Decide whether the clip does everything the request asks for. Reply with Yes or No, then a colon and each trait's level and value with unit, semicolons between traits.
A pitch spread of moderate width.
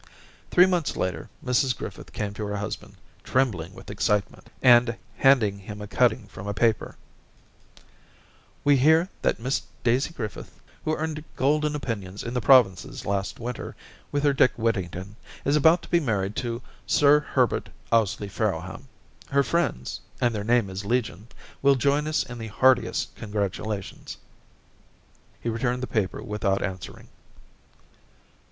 Yes: average, 5.0 semitones